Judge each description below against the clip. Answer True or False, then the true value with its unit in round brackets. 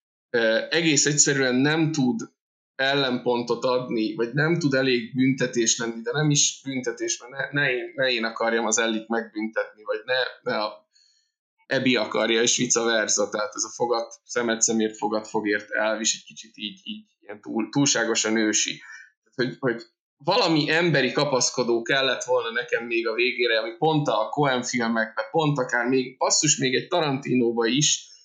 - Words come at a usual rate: False (165 wpm)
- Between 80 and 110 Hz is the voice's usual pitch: False (125 Hz)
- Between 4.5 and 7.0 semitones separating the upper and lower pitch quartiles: True (5.3 semitones)